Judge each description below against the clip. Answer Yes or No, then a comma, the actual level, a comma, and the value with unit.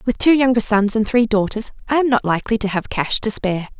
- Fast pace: Yes, fast, 255 wpm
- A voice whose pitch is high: Yes, high, 225 Hz